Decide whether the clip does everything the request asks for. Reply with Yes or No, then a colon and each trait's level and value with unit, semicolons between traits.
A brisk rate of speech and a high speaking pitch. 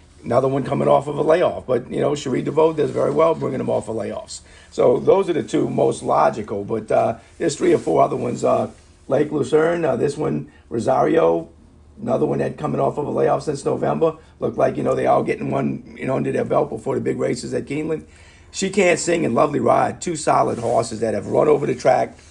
No: fast, 230 wpm; low, 135 Hz